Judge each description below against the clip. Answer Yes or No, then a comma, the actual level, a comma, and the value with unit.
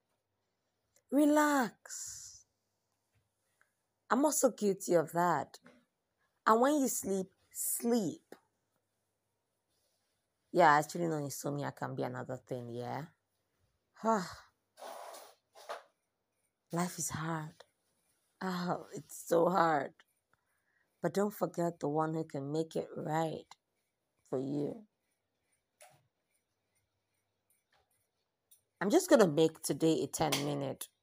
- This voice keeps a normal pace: No, slow, 90 wpm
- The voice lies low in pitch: No, medium, 160 Hz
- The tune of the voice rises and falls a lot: Yes, wide, 6.8 semitones